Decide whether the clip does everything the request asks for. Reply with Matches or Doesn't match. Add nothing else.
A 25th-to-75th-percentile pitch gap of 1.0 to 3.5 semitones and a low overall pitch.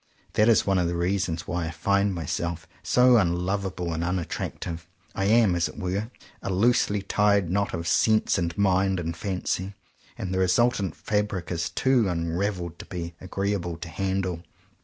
Matches